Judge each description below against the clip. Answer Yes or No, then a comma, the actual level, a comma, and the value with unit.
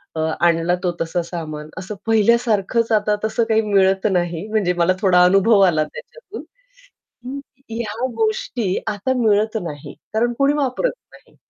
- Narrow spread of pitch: No, average, 4.6 semitones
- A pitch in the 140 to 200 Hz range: No, high, 210 Hz